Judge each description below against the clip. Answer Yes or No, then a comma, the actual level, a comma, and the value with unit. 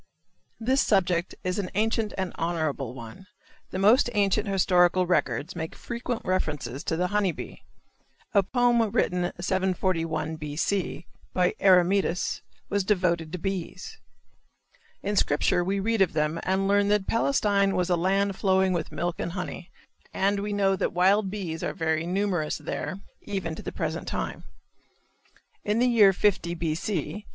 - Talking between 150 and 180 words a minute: Yes, average, 155 wpm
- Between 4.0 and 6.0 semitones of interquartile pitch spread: No, average, 2.9 semitones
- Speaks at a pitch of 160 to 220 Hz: Yes, high, 190 Hz